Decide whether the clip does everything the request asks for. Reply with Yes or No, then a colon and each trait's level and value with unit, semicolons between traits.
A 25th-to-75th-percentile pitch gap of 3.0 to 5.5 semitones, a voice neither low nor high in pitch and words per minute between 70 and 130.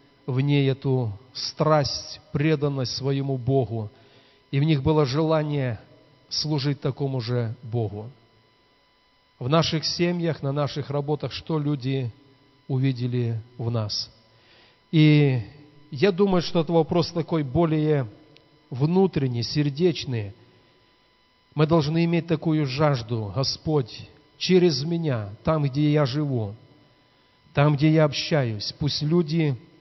Yes: average, 3.8 semitones; medium, 145 Hz; slow, 110 wpm